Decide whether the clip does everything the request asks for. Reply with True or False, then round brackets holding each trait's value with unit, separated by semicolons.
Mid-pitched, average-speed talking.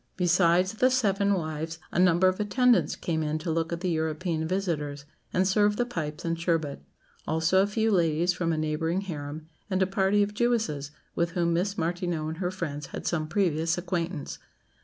True (170 Hz; 185 wpm)